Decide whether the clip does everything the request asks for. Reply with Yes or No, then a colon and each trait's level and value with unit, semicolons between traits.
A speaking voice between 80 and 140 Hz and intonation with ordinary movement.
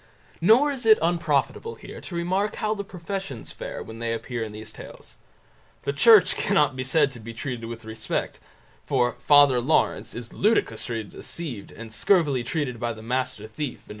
No: low, 135 Hz; wide, 7.1 semitones